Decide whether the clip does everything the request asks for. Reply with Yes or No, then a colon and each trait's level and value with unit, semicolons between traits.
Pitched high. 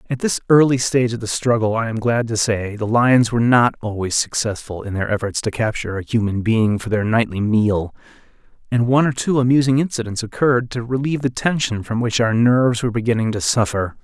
No: low, 115 Hz